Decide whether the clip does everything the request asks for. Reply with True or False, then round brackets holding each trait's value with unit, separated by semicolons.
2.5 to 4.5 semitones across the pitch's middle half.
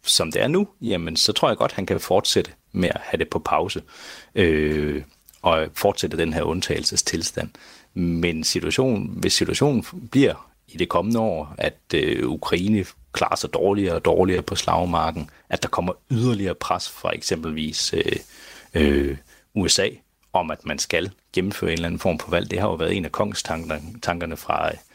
True (4.1 semitones)